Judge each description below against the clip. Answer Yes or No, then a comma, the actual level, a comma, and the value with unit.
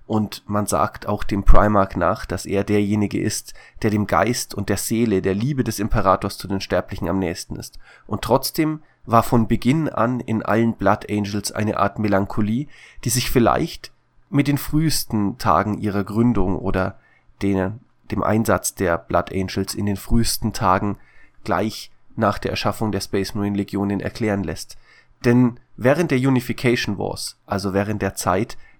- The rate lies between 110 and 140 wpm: No, average, 165 wpm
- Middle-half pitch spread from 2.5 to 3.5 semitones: Yes, average, 2.9 semitones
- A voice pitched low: Yes, low, 105 Hz